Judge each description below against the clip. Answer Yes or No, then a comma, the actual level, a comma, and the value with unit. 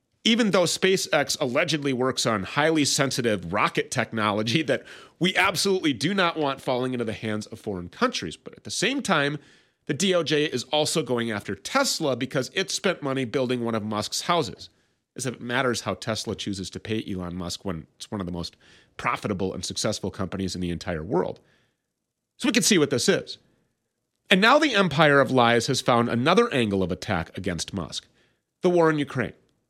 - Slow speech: No, average, 190 wpm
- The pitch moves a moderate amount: No, wide, 6.7 semitones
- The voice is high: No, low, 125 Hz